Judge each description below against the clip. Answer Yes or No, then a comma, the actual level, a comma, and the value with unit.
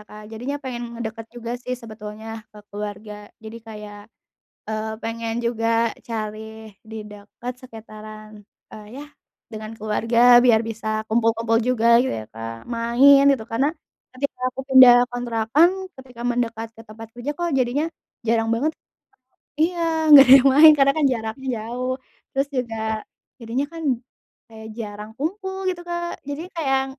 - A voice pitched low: No, high, 230 Hz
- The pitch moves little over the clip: No, average, 3.3 semitones